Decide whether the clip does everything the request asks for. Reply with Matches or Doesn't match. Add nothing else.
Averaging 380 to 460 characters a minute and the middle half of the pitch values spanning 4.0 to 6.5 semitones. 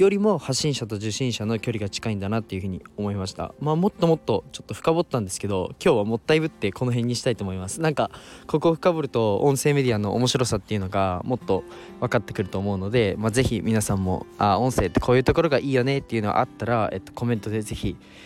Doesn't match